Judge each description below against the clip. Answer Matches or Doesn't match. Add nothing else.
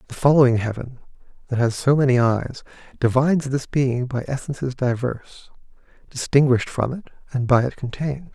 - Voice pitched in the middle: Doesn't match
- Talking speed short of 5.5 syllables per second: Doesn't match